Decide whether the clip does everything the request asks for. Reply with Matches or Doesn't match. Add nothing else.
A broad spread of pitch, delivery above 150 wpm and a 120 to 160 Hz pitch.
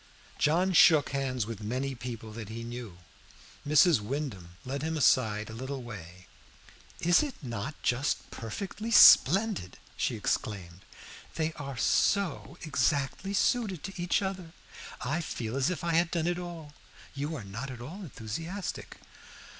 Doesn't match